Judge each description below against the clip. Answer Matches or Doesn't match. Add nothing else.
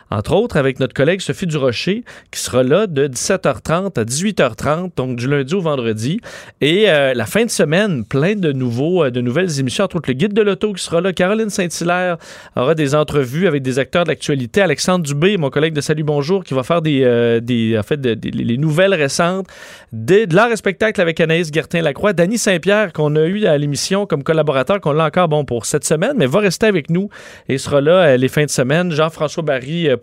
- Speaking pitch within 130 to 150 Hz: Doesn't match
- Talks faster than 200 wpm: Matches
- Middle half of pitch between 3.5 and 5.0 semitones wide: Doesn't match